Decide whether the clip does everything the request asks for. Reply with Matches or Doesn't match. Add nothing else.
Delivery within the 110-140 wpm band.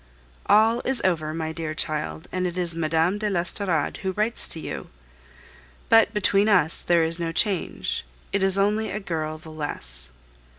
Doesn't match